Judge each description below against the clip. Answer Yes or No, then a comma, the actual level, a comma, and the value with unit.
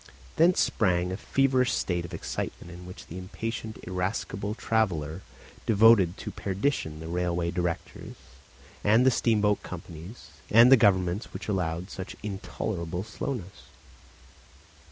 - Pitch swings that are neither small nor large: Yes, average, 4.1 semitones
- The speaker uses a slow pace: Yes, slow, 125 wpm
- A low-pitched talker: Yes, very low, 95 Hz